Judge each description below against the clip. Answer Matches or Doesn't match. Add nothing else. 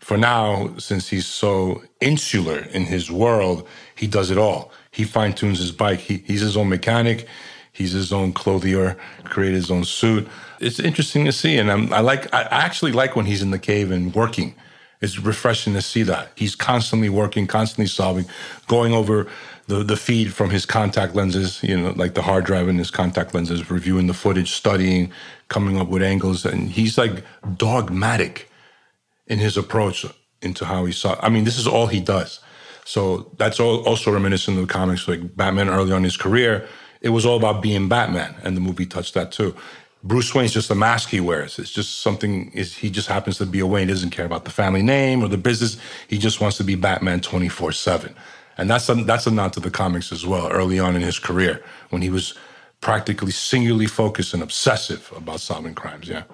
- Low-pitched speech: Matches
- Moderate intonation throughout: Matches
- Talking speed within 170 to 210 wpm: Matches